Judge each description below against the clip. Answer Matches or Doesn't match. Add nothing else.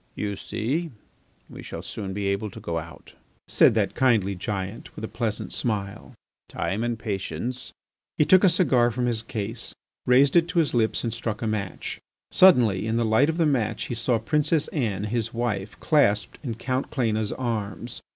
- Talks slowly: Doesn't match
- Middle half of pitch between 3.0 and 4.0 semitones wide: Matches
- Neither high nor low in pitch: Doesn't match